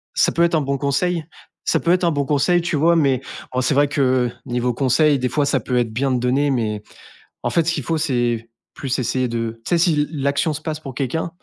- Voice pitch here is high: No, medium, 140 Hz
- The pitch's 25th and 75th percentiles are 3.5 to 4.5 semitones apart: Yes, average, 3.9 semitones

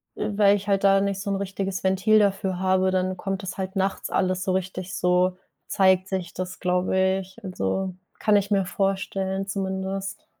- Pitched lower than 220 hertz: Yes, high, 190 Hz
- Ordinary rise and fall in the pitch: No, narrow, 0.9 semitones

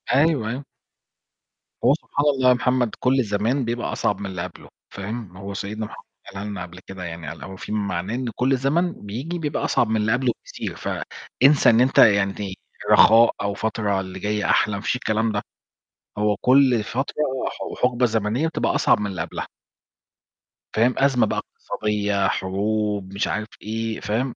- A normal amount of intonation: Yes, average, 3.9 semitones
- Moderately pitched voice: No, low, 110 Hz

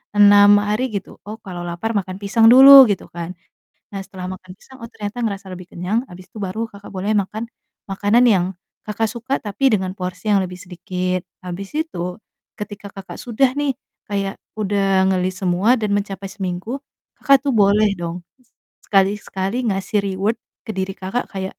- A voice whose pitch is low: No, high, 200 Hz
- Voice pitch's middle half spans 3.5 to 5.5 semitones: No, average, 2.8 semitones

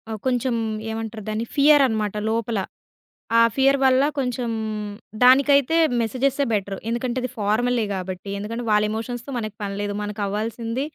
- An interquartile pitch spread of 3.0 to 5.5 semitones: Yes, average, 3.3 semitones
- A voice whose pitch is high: Yes, high, 230 Hz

